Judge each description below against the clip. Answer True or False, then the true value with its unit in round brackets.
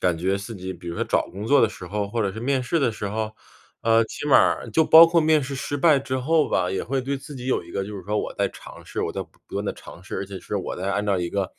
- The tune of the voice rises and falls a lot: True (6.0 semitones)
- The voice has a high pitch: False (110 Hz)